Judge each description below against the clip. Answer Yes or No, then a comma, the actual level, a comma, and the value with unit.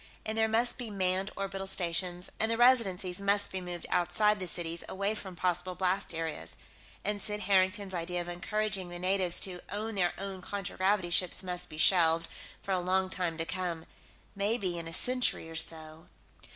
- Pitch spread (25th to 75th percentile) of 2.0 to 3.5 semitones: Yes, narrow, 2.4 semitones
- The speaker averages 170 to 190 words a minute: Yes, average, 180 wpm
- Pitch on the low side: No, medium, 185 Hz